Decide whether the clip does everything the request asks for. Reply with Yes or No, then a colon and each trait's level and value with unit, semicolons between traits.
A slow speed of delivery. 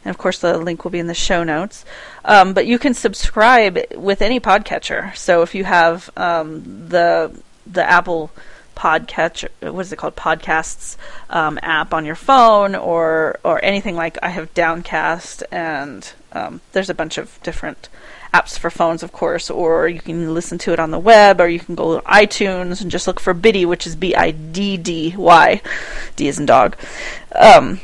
No: average, 185 wpm